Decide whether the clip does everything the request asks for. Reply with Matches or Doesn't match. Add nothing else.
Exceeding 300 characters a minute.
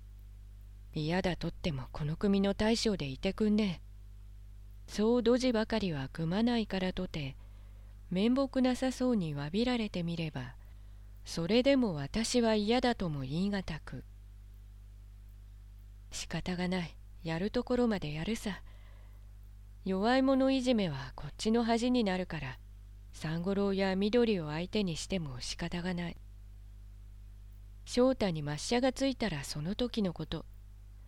Doesn't match